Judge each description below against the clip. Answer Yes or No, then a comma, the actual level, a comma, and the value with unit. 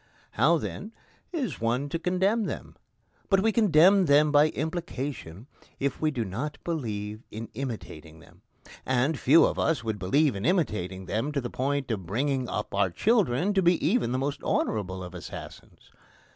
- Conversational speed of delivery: Yes, average, 170 wpm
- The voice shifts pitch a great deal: Yes, wide, 7.4 semitones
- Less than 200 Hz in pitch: Yes, medium, 140 Hz